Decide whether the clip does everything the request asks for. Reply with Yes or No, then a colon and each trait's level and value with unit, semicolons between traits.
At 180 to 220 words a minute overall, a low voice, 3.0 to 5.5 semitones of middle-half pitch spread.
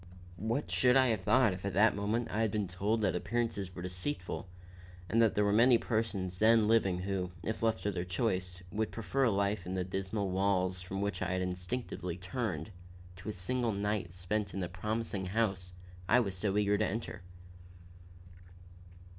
Yes: average, 185 wpm; low, 100 Hz; average, 3.3 semitones